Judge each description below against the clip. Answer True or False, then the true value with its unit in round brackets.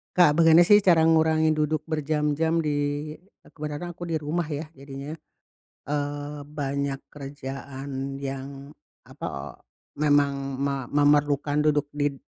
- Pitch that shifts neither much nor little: False (1.8 semitones)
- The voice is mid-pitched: True (145 Hz)